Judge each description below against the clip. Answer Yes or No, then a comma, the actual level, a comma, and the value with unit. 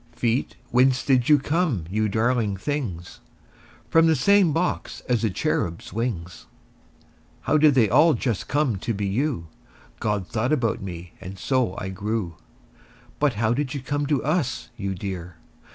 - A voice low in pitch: Yes, low, 120 Hz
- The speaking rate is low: No, average, 160 wpm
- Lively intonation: Yes, wide, 6.7 semitones